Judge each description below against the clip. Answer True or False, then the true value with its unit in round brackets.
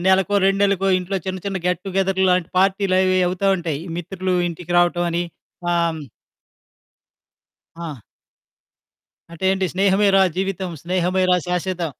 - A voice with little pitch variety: True (1.7 semitones)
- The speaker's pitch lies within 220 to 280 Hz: False (185 Hz)